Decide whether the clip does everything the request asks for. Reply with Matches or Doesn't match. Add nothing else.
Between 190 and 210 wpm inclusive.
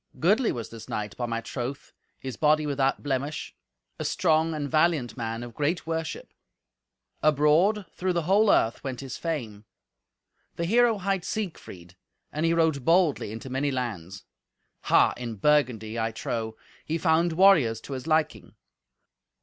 Doesn't match